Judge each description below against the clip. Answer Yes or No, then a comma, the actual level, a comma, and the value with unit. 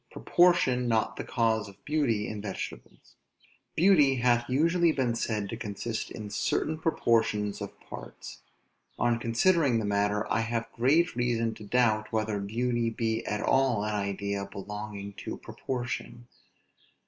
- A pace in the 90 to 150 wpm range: Yes, average, 140 wpm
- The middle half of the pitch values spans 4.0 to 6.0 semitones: No, average, 3.1 semitones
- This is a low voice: Yes, low, 115 Hz